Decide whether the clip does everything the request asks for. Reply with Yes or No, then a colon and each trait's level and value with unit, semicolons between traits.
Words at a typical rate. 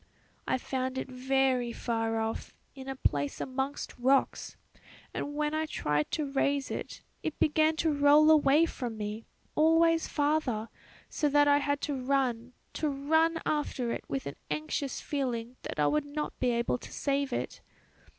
Yes: average, 165 wpm